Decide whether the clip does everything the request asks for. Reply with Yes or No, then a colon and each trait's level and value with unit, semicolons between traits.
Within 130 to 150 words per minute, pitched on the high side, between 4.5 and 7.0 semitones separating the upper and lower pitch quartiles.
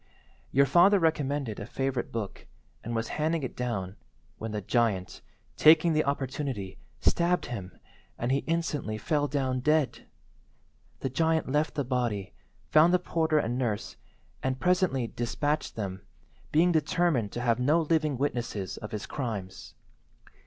No: average, 145 wpm; low, 135 Hz; average, 5.3 semitones